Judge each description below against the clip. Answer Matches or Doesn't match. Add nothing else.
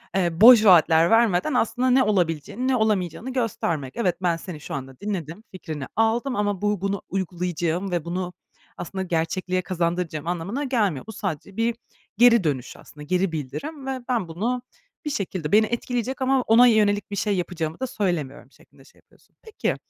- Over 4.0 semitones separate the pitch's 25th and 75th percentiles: Matches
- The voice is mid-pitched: Doesn't match